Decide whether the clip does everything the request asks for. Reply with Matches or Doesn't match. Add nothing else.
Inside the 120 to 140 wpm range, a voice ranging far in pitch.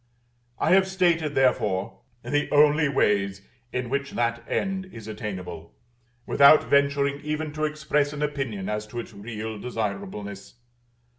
Matches